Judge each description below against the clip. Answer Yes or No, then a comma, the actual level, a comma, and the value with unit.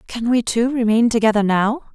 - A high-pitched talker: Yes, high, 230 Hz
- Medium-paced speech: Yes, average, 185 wpm